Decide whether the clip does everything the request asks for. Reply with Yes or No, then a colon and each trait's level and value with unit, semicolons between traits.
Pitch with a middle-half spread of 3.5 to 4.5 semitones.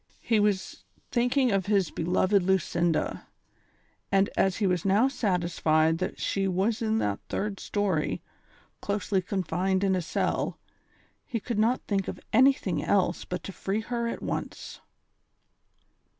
No: average, 3.1 semitones